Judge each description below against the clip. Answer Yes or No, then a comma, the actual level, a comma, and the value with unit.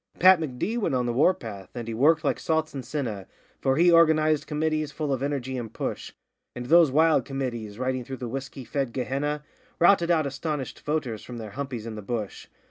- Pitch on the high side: No, low, 135 Hz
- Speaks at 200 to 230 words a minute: Yes, fast, 205 wpm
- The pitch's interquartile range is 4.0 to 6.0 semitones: Yes, average, 4.3 semitones